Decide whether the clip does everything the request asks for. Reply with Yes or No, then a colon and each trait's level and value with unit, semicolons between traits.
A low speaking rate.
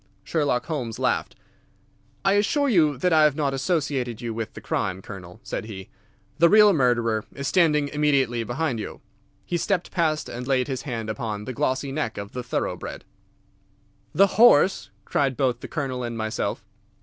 No: average, 170 wpm